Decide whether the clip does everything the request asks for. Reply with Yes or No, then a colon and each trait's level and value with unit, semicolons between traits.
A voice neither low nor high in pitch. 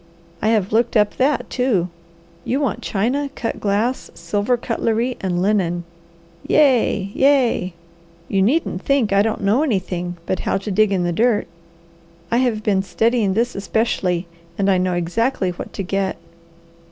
No: high, 210 Hz